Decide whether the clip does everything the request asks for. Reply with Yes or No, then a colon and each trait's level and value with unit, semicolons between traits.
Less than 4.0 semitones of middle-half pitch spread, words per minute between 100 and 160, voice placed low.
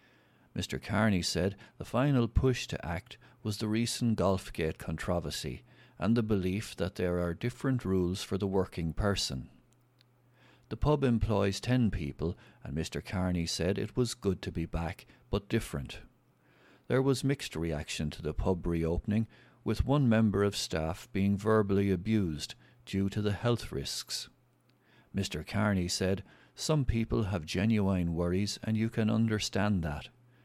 No: average, 4.4 semitones; average, 150 wpm; low, 100 Hz